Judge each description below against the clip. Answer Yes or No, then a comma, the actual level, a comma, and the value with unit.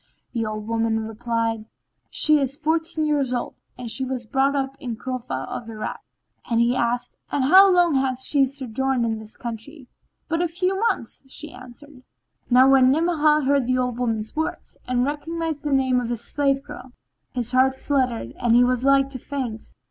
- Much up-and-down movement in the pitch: No, average, 3.3 semitones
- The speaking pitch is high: Yes, very high, 260 Hz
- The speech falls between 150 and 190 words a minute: Yes, average, 180 wpm